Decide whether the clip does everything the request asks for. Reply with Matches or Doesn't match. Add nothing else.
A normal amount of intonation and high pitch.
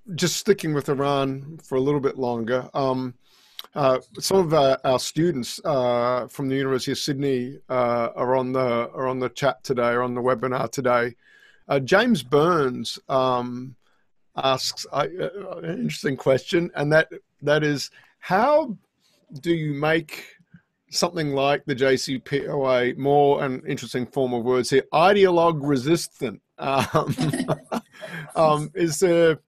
Doesn't match